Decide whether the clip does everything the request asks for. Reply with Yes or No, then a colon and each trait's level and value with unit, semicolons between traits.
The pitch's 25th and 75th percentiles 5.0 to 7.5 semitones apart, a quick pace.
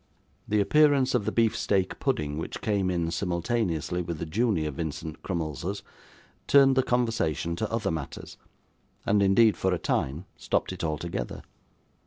No: wide, 5.5 semitones; average, 150 wpm